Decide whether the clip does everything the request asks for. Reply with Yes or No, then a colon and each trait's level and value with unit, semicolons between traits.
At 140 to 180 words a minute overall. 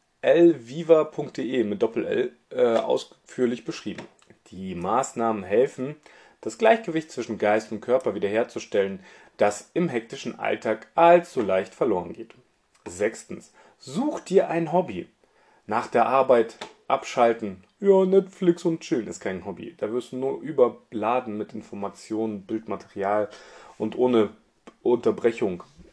No: slow, 125 wpm